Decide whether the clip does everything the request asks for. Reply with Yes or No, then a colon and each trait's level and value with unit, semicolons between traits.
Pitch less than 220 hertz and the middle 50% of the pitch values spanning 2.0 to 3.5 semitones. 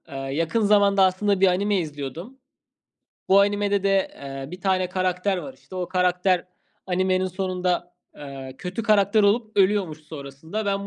Yes: medium, 185 Hz; average, 2.7 semitones